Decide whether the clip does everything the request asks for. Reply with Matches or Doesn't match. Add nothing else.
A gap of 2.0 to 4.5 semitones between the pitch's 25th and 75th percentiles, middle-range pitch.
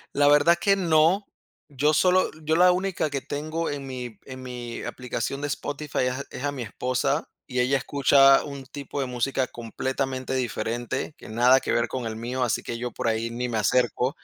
Doesn't match